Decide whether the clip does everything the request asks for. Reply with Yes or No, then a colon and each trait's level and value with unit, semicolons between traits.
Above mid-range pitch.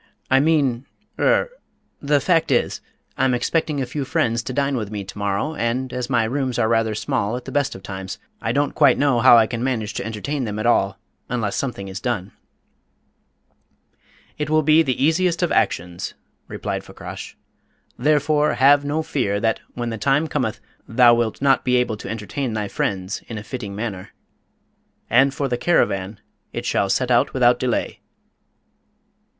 No: low, 125 Hz